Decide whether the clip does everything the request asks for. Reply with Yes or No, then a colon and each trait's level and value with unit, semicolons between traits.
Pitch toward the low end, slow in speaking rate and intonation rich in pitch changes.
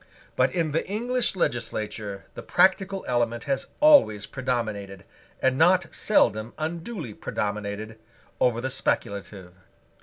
Yes: low, 125 Hz; slow, 115 wpm; wide, 8.3 semitones